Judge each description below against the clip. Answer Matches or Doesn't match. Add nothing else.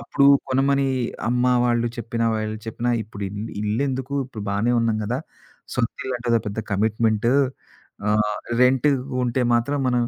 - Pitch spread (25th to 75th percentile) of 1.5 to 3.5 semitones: Matches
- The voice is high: Doesn't match